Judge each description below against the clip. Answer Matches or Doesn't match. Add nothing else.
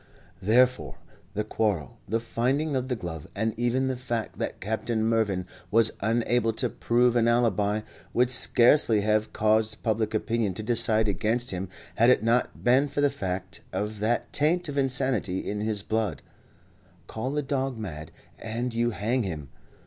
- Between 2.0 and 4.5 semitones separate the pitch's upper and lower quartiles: Matches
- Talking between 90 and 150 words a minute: Doesn't match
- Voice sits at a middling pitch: Doesn't match